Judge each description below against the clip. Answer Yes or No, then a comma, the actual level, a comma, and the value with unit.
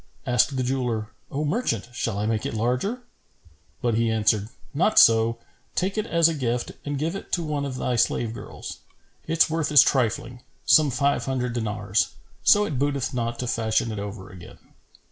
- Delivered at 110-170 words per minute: No, average, 185 wpm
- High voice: No, low, 125 Hz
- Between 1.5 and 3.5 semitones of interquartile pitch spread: No, average, 4.6 semitones